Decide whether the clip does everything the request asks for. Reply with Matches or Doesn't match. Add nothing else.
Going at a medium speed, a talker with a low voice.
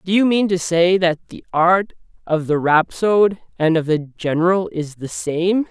Doesn't match